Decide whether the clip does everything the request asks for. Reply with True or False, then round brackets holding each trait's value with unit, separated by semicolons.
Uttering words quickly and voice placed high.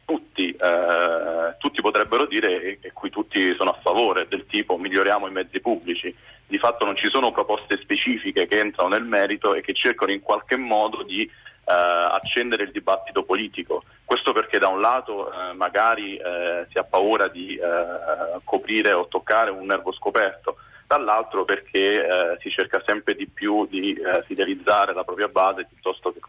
True (175 wpm; 315 Hz)